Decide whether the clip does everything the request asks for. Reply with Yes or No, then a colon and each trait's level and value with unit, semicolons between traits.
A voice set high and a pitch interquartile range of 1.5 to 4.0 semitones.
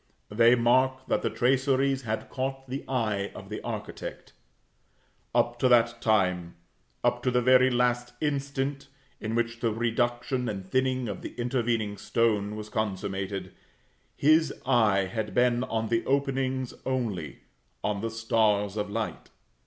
No: low, 120 Hz; average, 3.3 semitones